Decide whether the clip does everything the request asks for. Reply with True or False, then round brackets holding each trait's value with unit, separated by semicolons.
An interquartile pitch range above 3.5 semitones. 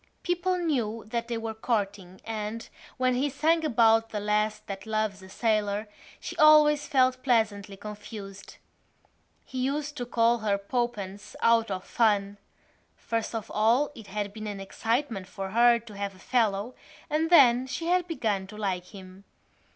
True (3.9 semitones)